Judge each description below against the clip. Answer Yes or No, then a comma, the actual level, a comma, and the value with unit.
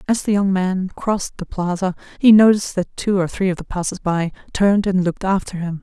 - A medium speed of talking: No, fast, 225 wpm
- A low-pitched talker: No, high, 190 Hz